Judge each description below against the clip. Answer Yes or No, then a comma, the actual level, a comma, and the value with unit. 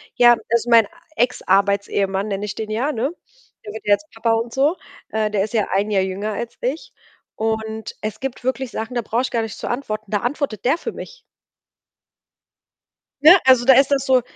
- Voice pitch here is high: Yes, high, 225 Hz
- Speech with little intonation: No, average, 3.4 semitones